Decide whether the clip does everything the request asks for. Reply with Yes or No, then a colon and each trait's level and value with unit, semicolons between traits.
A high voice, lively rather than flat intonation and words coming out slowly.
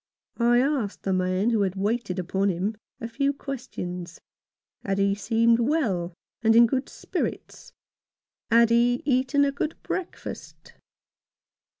No: high, 230 Hz; average, 4.8 semitones; slow, 130 wpm